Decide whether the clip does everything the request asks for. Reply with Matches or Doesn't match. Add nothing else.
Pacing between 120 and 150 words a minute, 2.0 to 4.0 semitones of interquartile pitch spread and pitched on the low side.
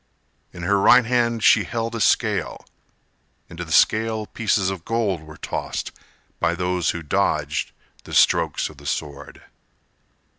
Doesn't match